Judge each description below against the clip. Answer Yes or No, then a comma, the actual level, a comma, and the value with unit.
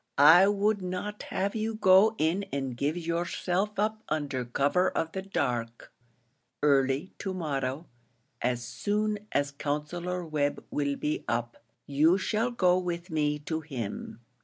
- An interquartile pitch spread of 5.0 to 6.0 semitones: Yes, average, 5.3 semitones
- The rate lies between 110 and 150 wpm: Yes, average, 140 wpm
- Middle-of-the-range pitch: Yes, medium, 165 Hz